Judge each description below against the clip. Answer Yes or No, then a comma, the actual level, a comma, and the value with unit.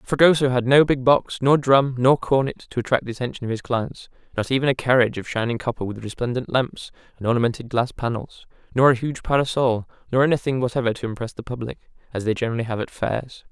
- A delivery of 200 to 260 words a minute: Yes, fast, 205 wpm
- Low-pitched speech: Yes, low, 125 Hz